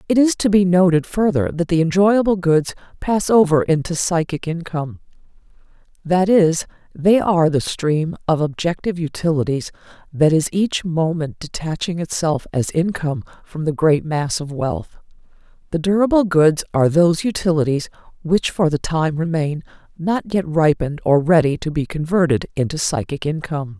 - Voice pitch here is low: No, medium, 165 Hz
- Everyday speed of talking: Yes, average, 150 wpm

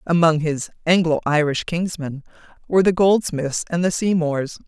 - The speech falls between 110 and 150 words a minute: Yes, average, 140 wpm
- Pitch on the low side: No, medium, 165 Hz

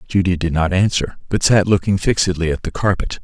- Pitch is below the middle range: Yes, very low, 90 Hz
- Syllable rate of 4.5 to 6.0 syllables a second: Yes, 5.8 syllables/s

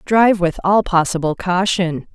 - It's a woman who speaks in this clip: Yes, female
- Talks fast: No, average, 140 wpm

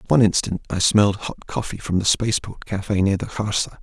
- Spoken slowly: No, fast, 205 wpm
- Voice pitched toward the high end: No, low, 100 Hz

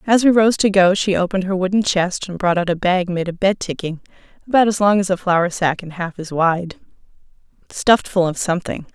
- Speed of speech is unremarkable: No, fast, 230 wpm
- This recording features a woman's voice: Yes, female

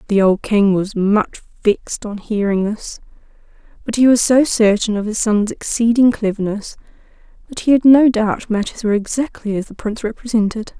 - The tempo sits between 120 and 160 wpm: No, average, 170 wpm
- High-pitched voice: Yes, high, 215 Hz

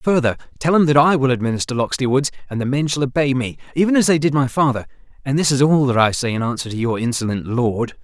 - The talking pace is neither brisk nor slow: No, fast, 255 wpm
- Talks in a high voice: No, low, 135 Hz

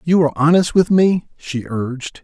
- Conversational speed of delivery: Yes, average, 190 wpm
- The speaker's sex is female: No, male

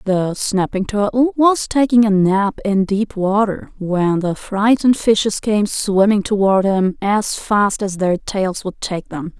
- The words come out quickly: No, average, 165 wpm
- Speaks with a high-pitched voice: Yes, high, 205 Hz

